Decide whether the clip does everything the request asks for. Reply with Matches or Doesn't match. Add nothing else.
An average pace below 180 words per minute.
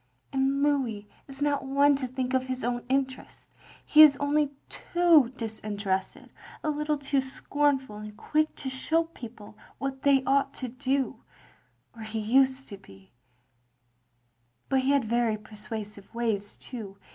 Matches